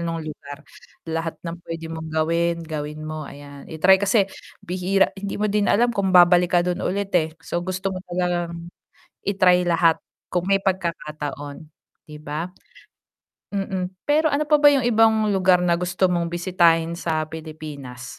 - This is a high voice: No, medium, 175 Hz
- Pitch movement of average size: Yes, average, 3.1 semitones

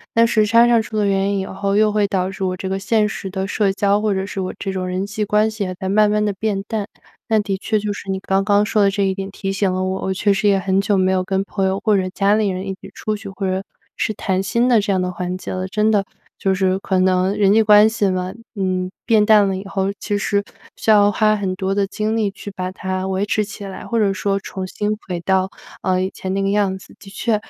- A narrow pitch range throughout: Yes, narrow, 1.7 semitones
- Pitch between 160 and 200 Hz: Yes, high, 195 Hz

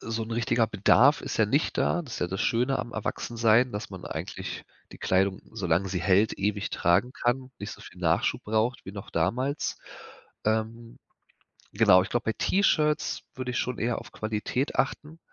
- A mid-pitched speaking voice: No, low, 115 Hz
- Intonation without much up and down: No, average, 3.9 semitones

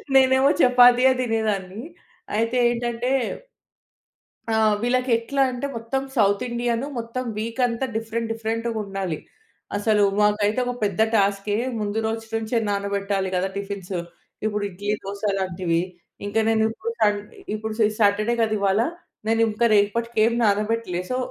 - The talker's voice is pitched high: Yes, high, 220 Hz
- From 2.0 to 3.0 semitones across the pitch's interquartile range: Yes, average, 2.7 semitones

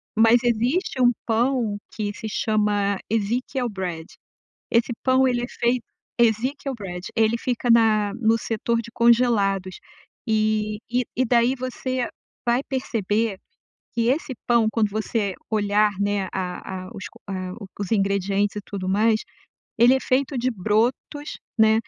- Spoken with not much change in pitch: No, average, 3.0 semitones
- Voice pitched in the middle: No, high, 225 Hz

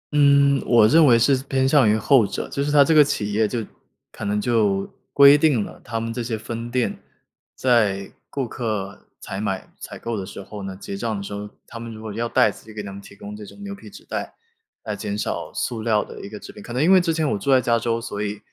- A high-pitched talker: No, low, 115 Hz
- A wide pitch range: No, average, 4.3 semitones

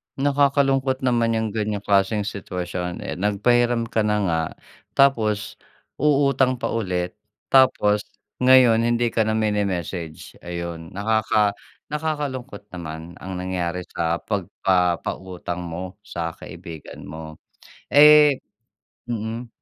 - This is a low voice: Yes, low, 105 Hz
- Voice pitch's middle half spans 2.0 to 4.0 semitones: No, wide, 5.4 semitones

